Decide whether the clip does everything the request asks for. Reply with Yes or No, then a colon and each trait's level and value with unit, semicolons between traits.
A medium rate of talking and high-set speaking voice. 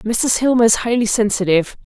Yes: average, 150 wpm; high, 225 Hz